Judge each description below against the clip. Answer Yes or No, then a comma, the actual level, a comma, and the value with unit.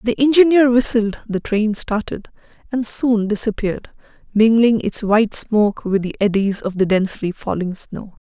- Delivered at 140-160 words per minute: Yes, average, 150 wpm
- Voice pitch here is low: No, high, 215 Hz